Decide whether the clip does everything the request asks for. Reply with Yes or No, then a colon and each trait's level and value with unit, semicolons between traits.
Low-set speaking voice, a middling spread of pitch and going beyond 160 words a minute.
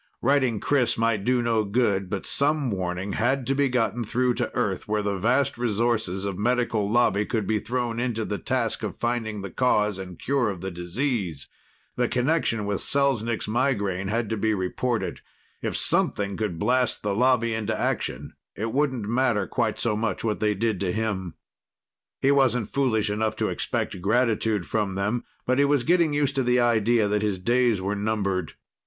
Yes: low, 110 Hz; average, 3.4 semitones; average, 185 wpm